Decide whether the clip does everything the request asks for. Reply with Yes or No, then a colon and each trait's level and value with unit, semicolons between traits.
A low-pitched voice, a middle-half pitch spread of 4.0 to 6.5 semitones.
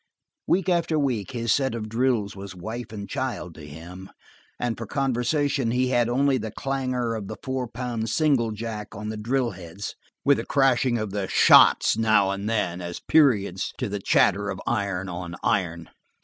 Yes: low, 115 Hz; average, 4.4 semitones